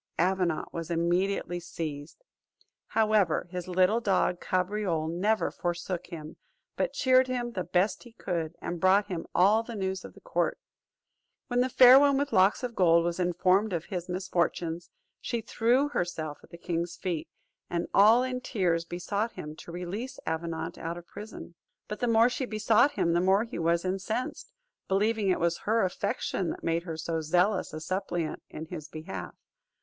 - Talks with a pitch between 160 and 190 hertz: Yes, medium, 185 Hz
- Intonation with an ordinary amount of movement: Yes, average, 4.2 semitones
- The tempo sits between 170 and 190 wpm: Yes, average, 175 wpm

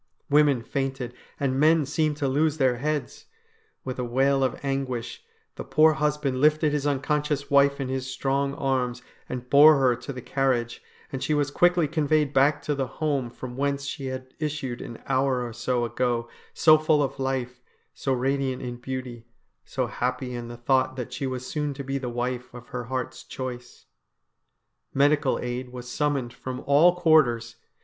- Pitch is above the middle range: No, low, 135 Hz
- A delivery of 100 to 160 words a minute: No, average, 180 wpm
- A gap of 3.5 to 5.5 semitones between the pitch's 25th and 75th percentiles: No, narrow, 2.5 semitones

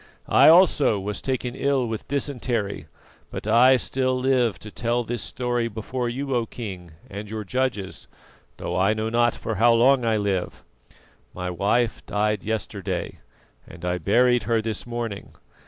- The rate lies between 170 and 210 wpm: No, average, 155 wpm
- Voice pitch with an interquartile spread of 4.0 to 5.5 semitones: No, average, 3.3 semitones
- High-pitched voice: No, low, 115 Hz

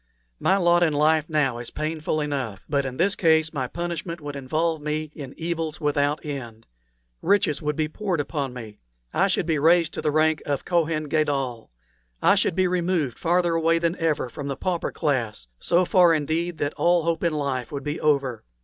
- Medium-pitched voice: Yes, medium, 155 Hz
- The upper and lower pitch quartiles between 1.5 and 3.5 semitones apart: Yes, average, 3.0 semitones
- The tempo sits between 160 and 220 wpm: Yes, average, 195 wpm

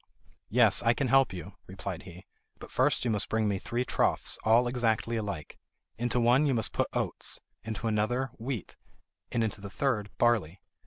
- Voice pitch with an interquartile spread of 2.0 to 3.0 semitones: Yes, narrow, 2.6 semitones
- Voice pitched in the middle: No, low, 115 Hz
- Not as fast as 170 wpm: No, average, 175 wpm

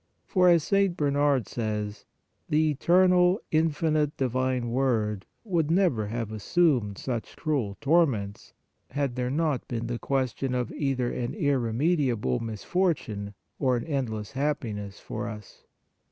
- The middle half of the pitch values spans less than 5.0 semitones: No, wide, 5.5 semitones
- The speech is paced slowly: Yes, slow, 130 wpm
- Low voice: Yes, low, 130 Hz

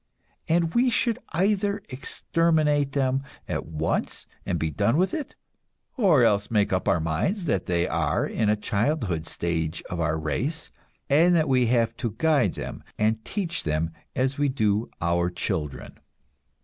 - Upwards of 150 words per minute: Yes, average, 160 wpm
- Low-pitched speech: Yes, low, 120 Hz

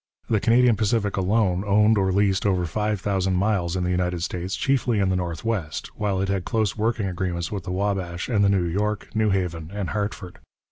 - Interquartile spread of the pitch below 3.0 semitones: Yes, narrow, 2.6 semitones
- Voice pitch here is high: No, low, 100 Hz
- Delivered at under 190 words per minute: No, average, 200 wpm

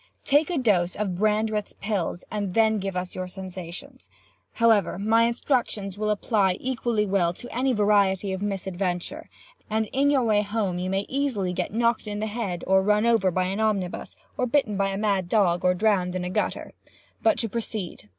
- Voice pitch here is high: Yes, high, 205 Hz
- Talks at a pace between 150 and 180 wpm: No, average, 190 wpm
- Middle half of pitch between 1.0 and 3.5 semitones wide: Yes, average, 3.2 semitones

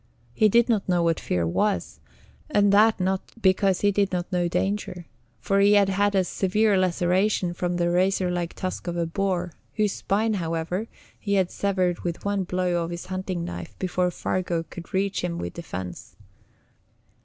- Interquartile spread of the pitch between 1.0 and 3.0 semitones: Yes, narrow, 2.4 semitones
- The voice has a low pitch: No, medium, 185 Hz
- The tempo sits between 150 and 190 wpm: Yes, average, 175 wpm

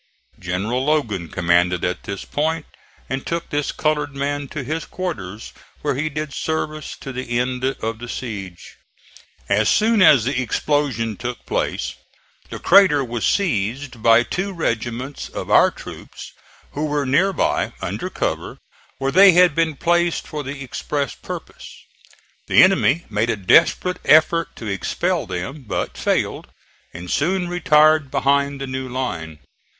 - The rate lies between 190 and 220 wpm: No, average, 150 wpm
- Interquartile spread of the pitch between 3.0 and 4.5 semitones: No, average, 5.3 semitones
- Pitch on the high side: No, low, 135 Hz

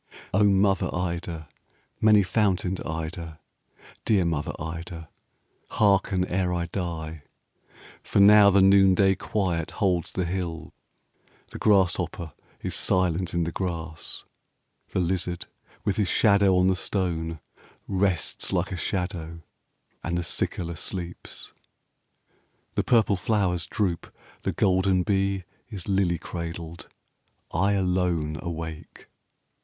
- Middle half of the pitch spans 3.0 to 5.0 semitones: No, narrow, 2.5 semitones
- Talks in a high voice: No, very low, 90 Hz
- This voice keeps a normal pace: No, slow, 115 wpm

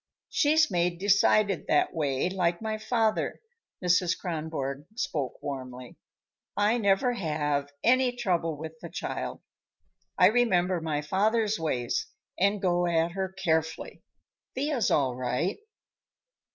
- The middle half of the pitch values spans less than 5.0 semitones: No, average, 5.3 semitones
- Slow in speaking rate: Yes, slow, 120 wpm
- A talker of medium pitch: Yes, medium, 175 Hz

